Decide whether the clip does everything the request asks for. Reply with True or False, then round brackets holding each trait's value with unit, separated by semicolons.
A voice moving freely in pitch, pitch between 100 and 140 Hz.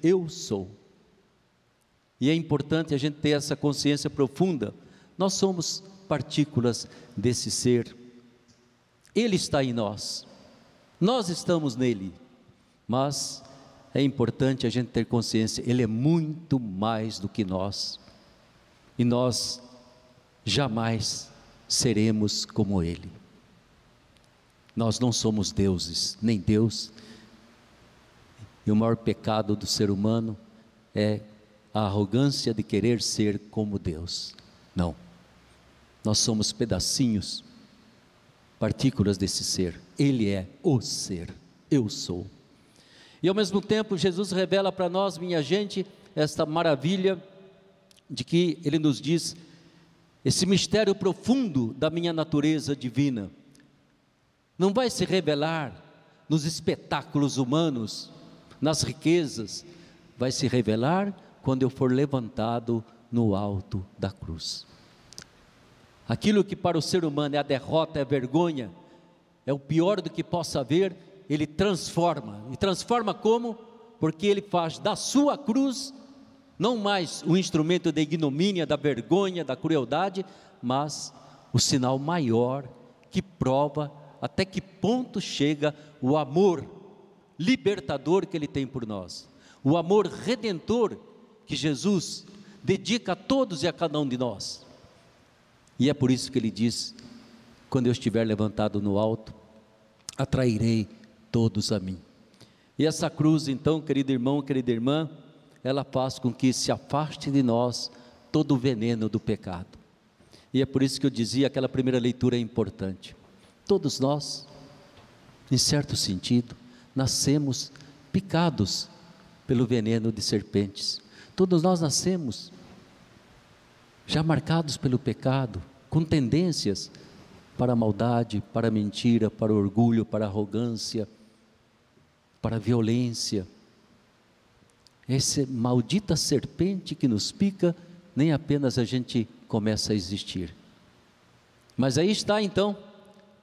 True (6.7 semitones; 135 Hz)